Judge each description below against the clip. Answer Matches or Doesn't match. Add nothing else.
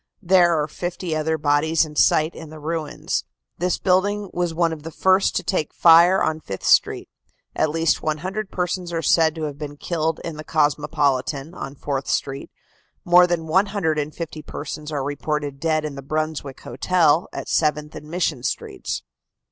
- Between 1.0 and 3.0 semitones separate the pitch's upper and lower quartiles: Matches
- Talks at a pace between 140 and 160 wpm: Doesn't match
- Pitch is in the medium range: Matches